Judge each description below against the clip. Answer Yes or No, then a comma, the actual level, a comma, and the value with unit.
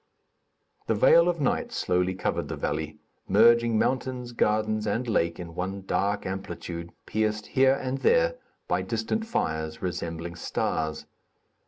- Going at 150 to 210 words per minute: No, slow, 135 wpm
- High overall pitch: No, low, 105 Hz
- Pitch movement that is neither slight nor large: No, wide, 6.6 semitones